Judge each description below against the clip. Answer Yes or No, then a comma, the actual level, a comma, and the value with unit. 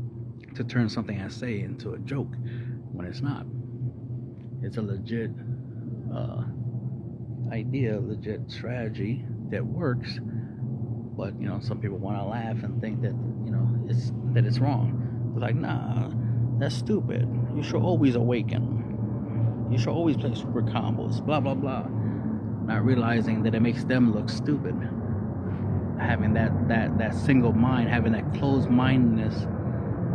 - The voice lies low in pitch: Yes, low, 120 Hz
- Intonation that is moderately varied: No, narrow, 1.4 semitones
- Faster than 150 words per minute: No, average, 145 wpm